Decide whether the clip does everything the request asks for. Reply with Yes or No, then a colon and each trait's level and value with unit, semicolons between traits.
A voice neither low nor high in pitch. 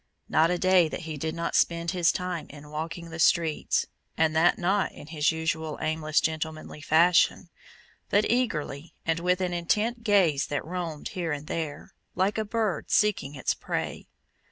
Yes: medium, 165 Hz